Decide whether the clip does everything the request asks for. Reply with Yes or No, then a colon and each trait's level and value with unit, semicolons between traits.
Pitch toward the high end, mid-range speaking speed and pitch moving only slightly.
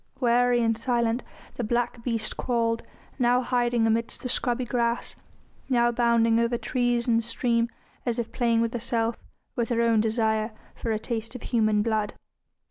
Yes: high, 235 Hz; average, 160 wpm; narrow, 1.1 semitones